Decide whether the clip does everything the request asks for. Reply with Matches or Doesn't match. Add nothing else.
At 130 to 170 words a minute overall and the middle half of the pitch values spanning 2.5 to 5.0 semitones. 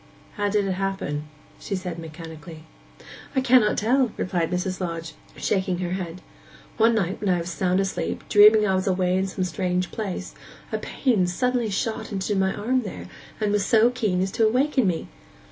Doesn't match